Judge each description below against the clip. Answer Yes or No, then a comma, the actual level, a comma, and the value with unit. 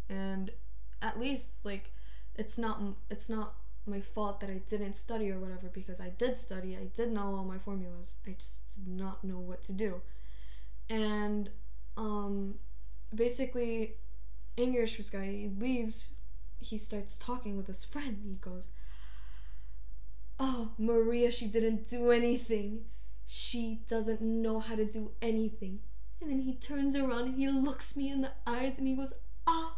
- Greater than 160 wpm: No, average, 155 wpm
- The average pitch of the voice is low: No, high, 215 Hz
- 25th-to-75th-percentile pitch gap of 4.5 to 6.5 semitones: No, average, 3.7 semitones